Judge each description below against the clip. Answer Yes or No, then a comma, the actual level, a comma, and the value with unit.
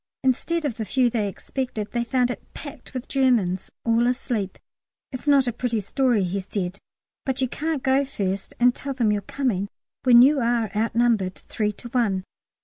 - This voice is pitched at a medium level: No, high, 240 Hz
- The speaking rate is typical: Yes, average, 180 wpm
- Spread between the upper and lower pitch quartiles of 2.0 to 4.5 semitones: Yes, average, 4.0 semitones